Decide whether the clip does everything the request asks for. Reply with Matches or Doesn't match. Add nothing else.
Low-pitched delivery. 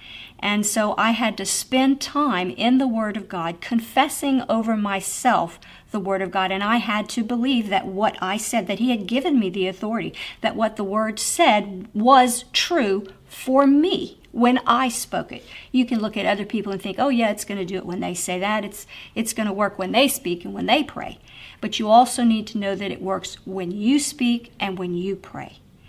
Doesn't match